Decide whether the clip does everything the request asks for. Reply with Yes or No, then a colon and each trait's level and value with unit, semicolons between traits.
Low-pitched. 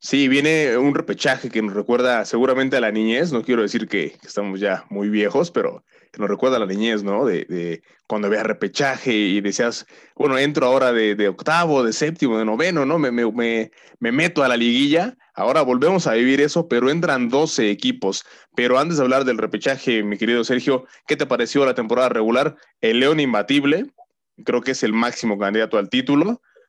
Yes: low, 125 Hz